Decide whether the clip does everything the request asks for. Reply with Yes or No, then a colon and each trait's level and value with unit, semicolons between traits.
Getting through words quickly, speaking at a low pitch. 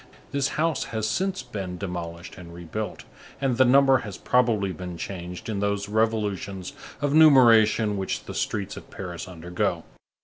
No: average, 150 wpm; low, 105 Hz